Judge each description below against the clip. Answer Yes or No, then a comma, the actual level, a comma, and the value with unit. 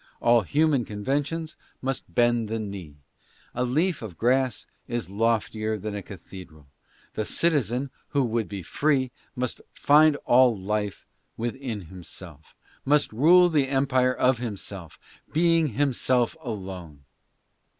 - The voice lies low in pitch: Yes, low, 120 Hz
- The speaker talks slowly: Yes, slow, 130 wpm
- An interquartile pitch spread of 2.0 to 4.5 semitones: No, average, 5.0 semitones